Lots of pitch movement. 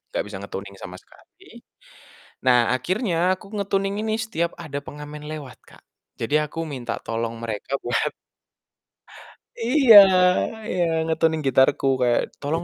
Yes: wide, 7.1 semitones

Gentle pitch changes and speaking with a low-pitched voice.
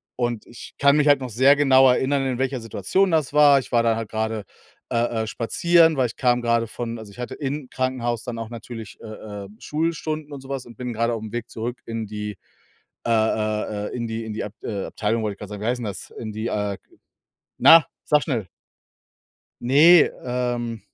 No: average, 3.3 semitones; low, 120 Hz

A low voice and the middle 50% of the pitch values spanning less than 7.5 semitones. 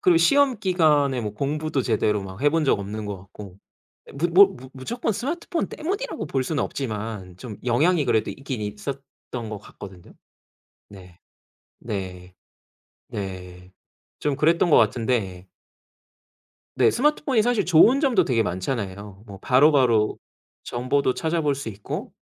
No: low, 125 Hz; wide, 8.0 semitones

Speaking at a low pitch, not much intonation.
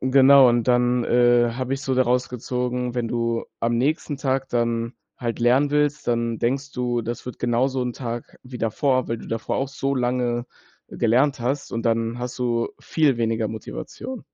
Yes: low, 125 Hz; narrow, 2.0 semitones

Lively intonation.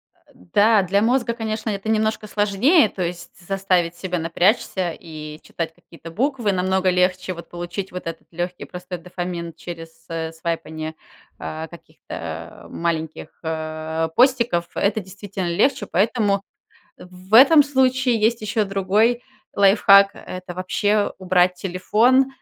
No: average, 4.0 semitones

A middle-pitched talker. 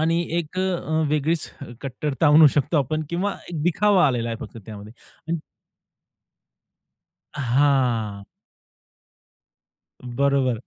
Yes: medium, 145 Hz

